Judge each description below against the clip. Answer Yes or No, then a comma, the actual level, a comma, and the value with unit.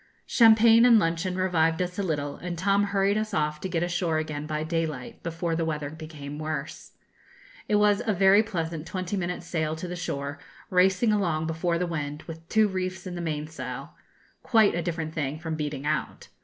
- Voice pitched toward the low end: No, medium, 170 Hz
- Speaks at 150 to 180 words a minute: No, average, 190 wpm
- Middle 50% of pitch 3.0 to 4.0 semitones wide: Yes, average, 3.4 semitones